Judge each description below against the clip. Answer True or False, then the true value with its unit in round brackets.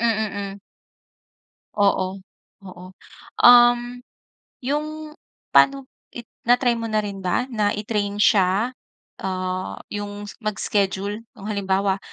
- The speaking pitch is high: True (205 Hz)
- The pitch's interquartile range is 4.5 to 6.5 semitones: False (3.6 semitones)